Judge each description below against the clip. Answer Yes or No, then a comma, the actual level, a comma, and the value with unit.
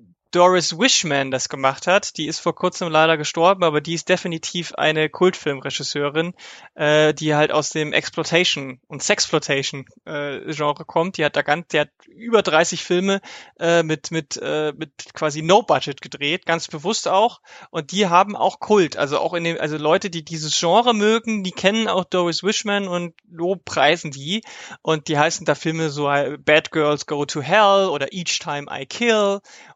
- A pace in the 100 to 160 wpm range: No, average, 175 wpm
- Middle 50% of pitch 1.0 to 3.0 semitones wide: No, average, 3.4 semitones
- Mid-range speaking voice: Yes, medium, 165 Hz